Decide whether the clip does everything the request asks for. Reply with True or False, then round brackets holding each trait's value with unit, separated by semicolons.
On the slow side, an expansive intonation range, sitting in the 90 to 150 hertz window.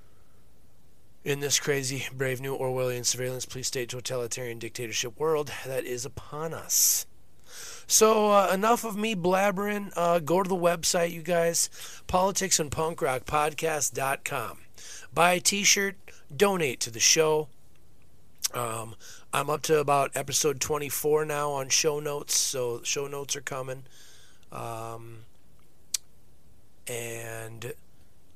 True (120 wpm; 5.8 semitones; 140 Hz)